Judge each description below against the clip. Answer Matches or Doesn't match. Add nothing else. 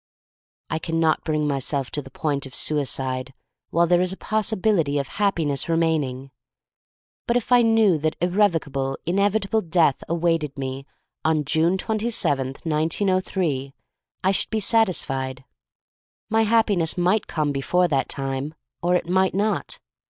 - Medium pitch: Matches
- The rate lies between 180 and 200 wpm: Doesn't match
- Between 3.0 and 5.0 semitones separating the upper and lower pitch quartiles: Doesn't match